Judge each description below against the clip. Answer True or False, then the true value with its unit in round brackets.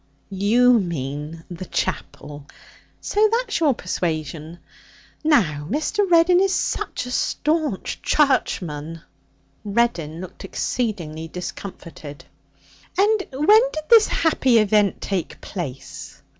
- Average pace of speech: False (100 wpm)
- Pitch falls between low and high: False (205 Hz)